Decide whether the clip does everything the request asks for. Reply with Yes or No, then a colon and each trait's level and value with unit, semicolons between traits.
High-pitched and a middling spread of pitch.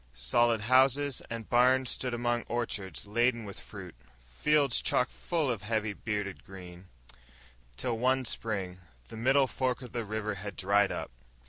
No: low, 115 Hz; average, 3.9 semitones